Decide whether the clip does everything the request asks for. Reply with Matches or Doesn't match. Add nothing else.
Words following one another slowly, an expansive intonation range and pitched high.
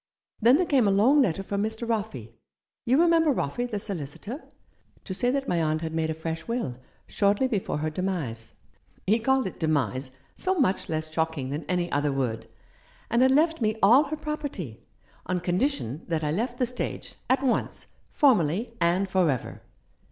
Doesn't match